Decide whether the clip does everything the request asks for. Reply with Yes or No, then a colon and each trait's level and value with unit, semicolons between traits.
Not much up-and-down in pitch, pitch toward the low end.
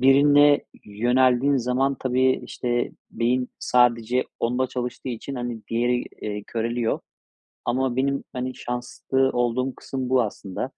Yes: narrow, 1.4 semitones; low, 125 Hz